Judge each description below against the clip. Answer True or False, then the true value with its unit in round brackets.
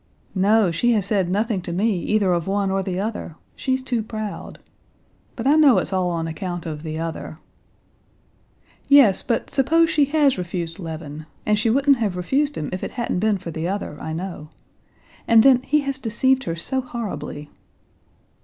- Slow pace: False (180 wpm)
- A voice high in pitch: True (205 Hz)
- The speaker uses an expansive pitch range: True (6.6 semitones)